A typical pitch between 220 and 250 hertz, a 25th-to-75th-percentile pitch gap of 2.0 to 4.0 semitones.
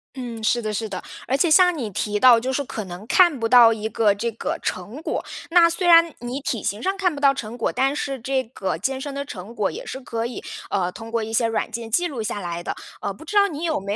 No: high, 240 Hz; average, 4.9 semitones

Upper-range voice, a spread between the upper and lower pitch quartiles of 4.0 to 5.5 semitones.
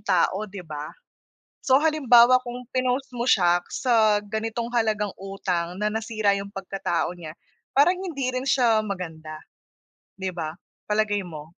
Yes: high, 210 Hz; average, 5.0 semitones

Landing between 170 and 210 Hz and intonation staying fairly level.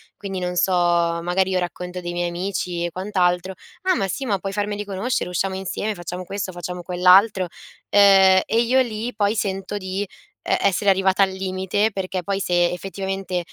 Yes: high, 190 Hz; narrow, 1.9 semitones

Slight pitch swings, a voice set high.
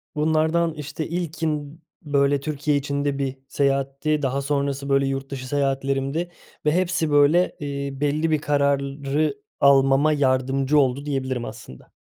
No: narrow, 1.8 semitones; medium, 140 Hz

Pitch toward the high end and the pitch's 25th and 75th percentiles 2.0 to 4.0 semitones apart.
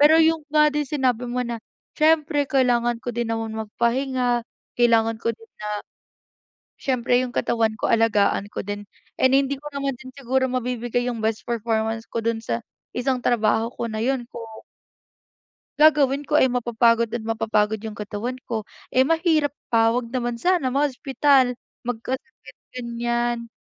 Yes: high, 240 Hz; average, 2.9 semitones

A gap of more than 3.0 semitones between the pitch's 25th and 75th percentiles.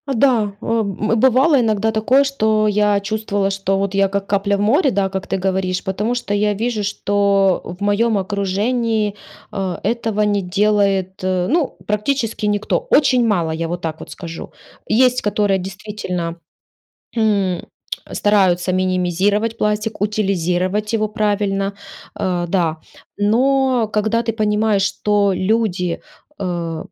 No: narrow, 2.4 semitones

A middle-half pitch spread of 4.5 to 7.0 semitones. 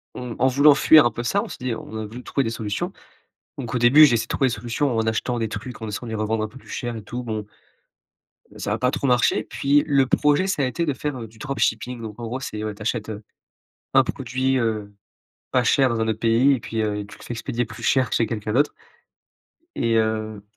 No: average, 3.2 semitones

